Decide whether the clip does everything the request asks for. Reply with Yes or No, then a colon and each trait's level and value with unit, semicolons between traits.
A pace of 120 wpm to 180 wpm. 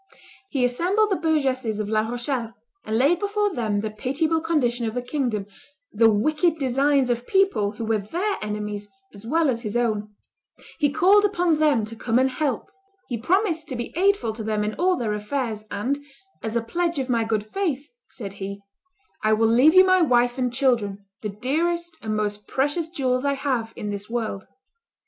No: average, 190 wpm